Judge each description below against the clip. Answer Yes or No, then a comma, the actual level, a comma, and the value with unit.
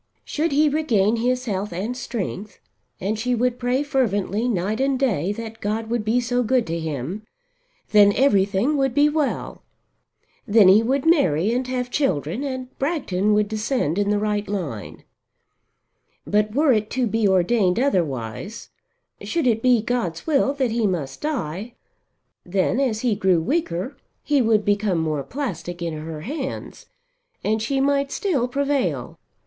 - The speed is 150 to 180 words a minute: Yes, average, 155 wpm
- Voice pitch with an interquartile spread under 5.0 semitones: No, average, 5.3 semitones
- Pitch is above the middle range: Yes, high, 225 Hz